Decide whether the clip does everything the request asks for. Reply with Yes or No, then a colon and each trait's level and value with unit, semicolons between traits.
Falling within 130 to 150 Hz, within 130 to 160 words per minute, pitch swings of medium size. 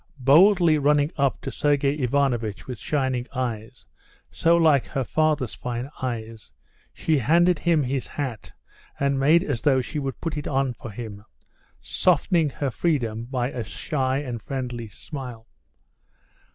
Yes: low, 135 Hz; average, 145 wpm; average, 3.5 semitones